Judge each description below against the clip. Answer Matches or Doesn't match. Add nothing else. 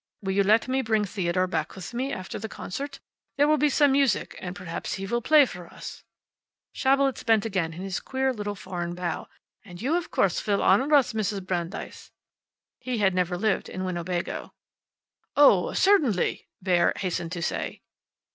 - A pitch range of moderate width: Doesn't match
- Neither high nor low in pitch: Doesn't match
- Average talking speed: Matches